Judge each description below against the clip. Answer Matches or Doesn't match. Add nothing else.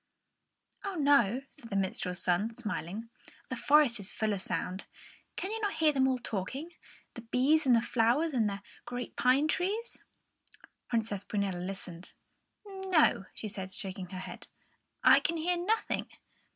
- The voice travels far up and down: Matches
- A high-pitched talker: Matches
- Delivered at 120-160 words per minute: Matches